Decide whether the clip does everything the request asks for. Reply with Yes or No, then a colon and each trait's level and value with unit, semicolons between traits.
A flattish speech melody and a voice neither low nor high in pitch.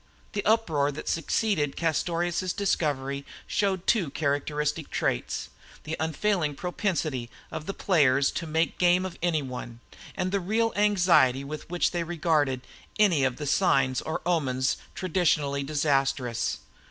No: average, 4.4 semitones; medium, 160 Hz